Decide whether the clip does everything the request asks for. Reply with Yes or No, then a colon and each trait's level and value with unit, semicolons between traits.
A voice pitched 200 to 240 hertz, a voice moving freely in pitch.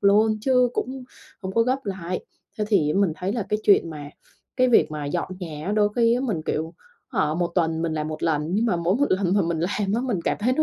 No: high, 190 Hz; wide, 5.8 semitones